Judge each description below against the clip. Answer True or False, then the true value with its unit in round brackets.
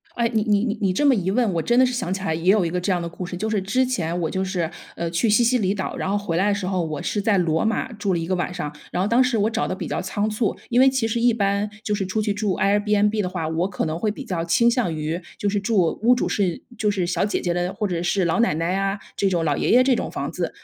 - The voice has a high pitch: True (195 Hz)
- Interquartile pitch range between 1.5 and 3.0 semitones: False (3.7 semitones)